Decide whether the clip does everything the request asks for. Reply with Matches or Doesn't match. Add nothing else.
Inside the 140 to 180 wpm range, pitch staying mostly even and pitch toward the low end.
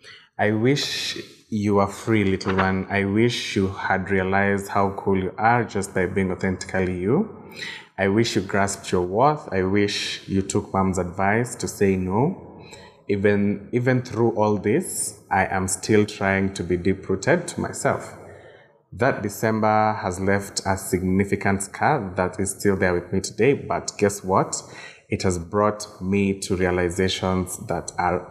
Matches